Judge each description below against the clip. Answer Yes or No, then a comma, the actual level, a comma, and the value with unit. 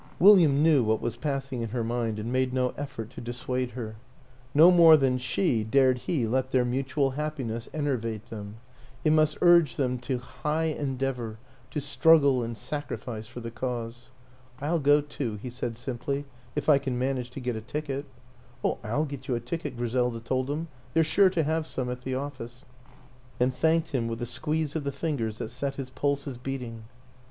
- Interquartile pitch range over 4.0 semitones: No, average, 3.2 semitones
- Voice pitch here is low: Yes, low, 130 Hz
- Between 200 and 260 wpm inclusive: Yes, fast, 205 wpm